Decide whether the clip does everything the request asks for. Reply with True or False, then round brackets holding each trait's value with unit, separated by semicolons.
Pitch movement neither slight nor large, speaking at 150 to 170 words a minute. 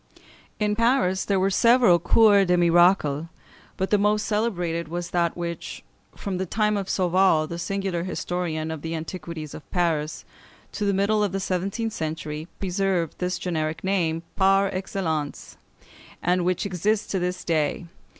True (3.0 semitones; 160 wpm)